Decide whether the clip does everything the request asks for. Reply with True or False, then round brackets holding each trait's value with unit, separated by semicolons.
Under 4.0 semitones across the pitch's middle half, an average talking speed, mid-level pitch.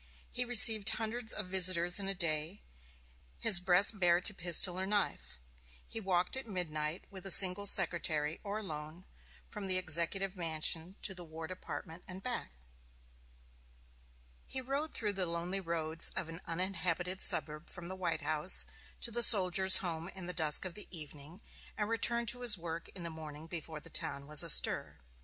True (3.2 semitones; 170 wpm; 180 Hz)